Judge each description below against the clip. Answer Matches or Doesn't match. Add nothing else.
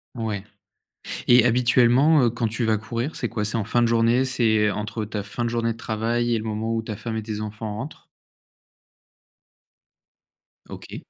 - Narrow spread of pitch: Matches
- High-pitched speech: Doesn't match